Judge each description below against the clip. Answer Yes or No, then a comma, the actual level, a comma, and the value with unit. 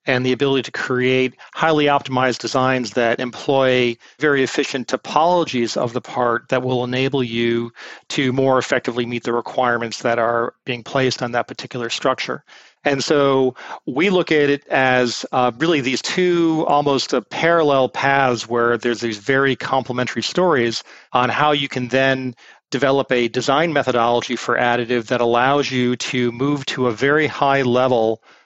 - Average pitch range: No, narrow, 2.3 semitones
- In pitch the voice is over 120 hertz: Yes, low, 130 Hz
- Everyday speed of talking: Yes, average, 160 wpm